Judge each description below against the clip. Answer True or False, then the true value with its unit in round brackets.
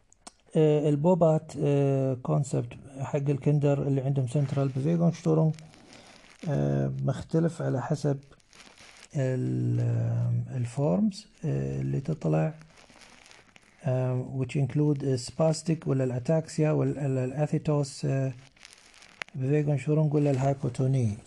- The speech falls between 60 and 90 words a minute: True (70 wpm)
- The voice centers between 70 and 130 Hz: False (140 Hz)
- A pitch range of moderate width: True (3.0 semitones)